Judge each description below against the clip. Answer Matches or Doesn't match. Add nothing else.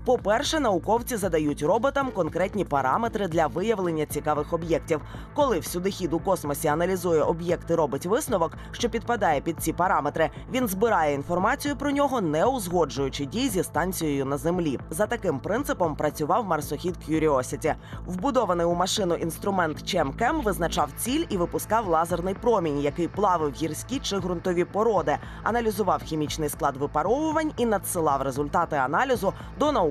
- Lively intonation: Matches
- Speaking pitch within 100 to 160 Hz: Doesn't match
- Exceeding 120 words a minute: Matches